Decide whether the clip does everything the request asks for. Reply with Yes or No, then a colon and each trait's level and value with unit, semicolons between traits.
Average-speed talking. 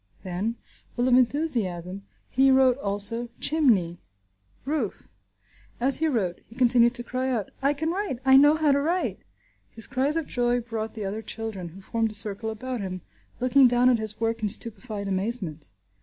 Yes: average, 175 wpm